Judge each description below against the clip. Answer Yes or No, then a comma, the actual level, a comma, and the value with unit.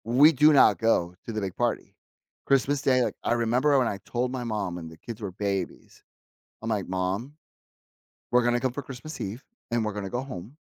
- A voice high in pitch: No, low, 120 Hz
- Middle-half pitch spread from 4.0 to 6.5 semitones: Yes, average, 4.6 semitones